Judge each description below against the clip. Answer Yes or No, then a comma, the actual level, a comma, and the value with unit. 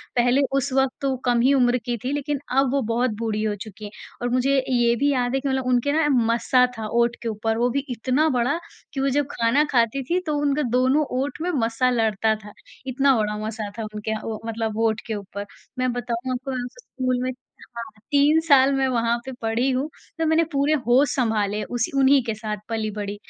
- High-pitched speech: Yes, high, 245 Hz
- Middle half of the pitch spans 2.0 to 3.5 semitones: Yes, average, 3.2 semitones